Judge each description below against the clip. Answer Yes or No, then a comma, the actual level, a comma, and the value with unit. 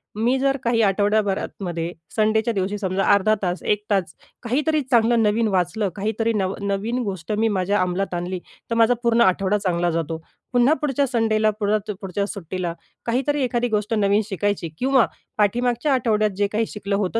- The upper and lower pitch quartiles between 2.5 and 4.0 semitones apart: Yes, average, 3.3 semitones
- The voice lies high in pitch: Yes, high, 210 Hz